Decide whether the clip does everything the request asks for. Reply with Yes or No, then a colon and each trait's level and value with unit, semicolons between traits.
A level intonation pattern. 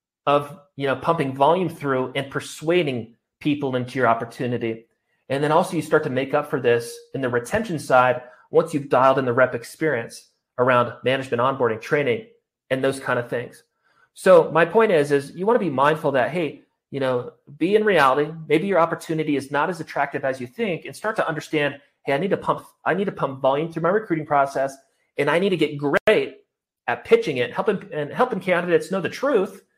No: average, 3.8 semitones